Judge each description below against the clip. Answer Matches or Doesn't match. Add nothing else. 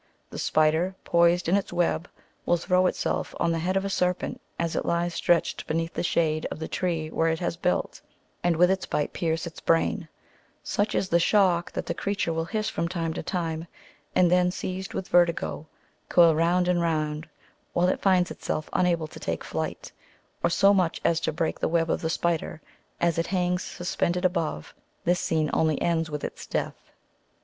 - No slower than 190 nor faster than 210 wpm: Matches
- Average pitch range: Doesn't match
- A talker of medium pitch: Matches